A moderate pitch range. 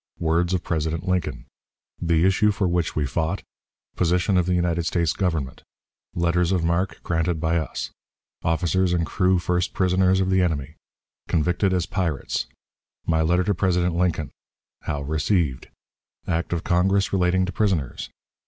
No: narrow, 2.1 semitones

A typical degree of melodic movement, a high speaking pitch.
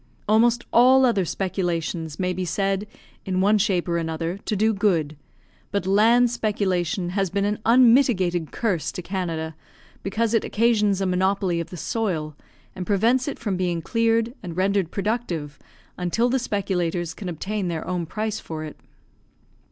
Yes: average, 3.9 semitones; high, 195 Hz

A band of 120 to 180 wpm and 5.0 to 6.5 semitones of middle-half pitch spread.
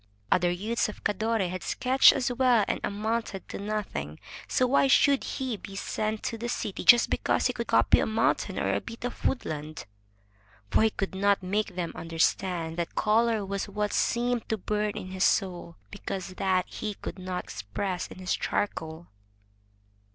No: average, 175 wpm; average, 3.6 semitones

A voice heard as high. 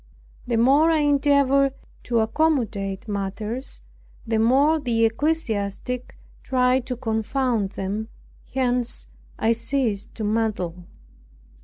Yes: high, 235 Hz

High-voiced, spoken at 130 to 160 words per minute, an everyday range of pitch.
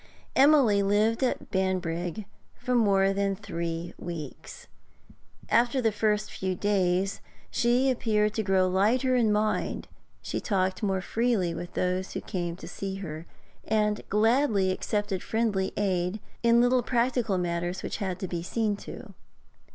Yes: high, 200 Hz; average, 145 wpm; average, 3.4 semitones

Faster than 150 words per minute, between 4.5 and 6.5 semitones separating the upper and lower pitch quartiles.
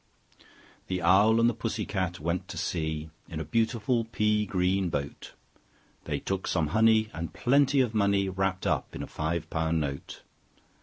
Yes: average, 165 wpm; average, 5.1 semitones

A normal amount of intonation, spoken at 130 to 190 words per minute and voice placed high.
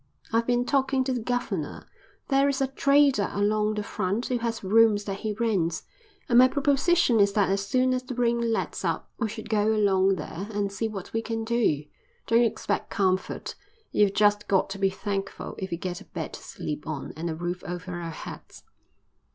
No: average, 3.8 semitones; average, 200 wpm; high, 215 Hz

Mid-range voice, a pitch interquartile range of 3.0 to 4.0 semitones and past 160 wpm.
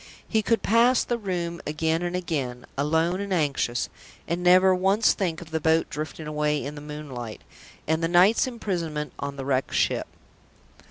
Yes: medium, 165 Hz; average, 3.6 semitones; average, 170 wpm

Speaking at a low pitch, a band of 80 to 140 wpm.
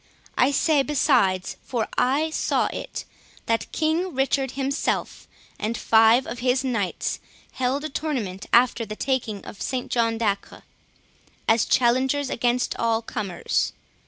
No: very high, 250 Hz; slow, 135 wpm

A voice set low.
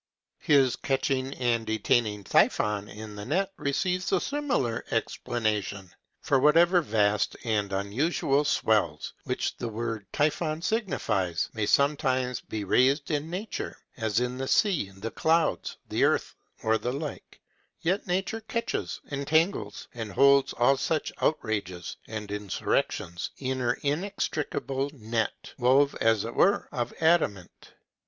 Yes: low, 130 Hz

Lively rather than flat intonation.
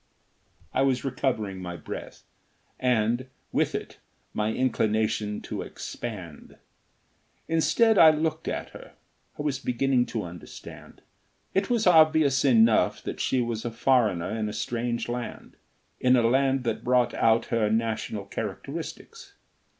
No: average, 3.6 semitones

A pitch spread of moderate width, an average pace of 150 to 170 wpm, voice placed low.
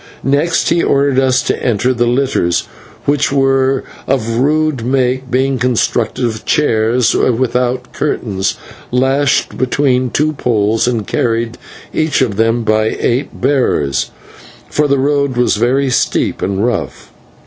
No: average, 3.0 semitones; slow, 135 wpm; low, 125 Hz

